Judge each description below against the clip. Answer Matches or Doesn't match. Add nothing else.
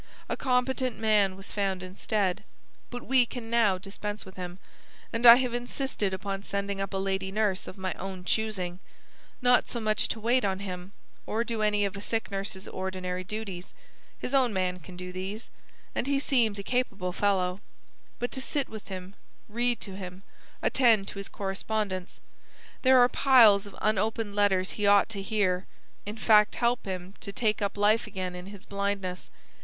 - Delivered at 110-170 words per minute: Doesn't match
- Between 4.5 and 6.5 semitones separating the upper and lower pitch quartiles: Doesn't match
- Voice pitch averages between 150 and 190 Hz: Doesn't match